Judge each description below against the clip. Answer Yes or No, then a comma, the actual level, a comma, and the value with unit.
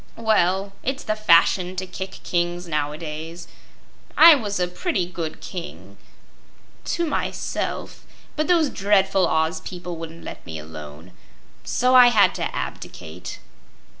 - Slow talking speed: Yes, slow, 130 wpm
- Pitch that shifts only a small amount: No, average, 4.8 semitones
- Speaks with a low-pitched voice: No, medium, 180 Hz